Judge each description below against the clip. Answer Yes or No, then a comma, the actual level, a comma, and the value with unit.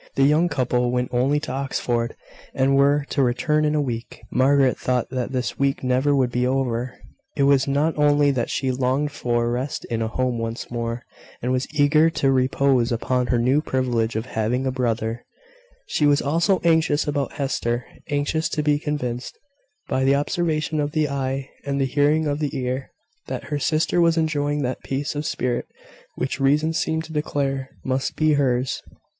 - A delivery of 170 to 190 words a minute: Yes, average, 185 wpm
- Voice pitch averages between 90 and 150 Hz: Yes, low, 135 Hz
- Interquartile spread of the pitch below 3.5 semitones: Yes, average, 2.8 semitones